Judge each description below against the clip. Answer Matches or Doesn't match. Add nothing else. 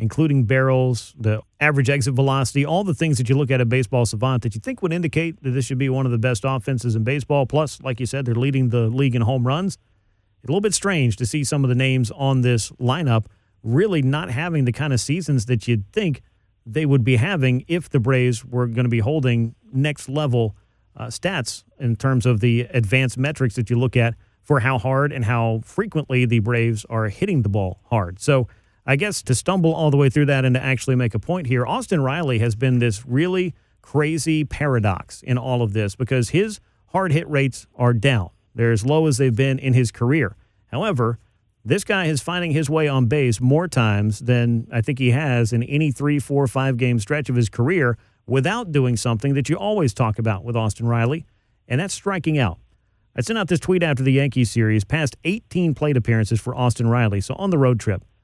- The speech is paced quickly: Matches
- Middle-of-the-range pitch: Doesn't match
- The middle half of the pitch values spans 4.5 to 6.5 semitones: Doesn't match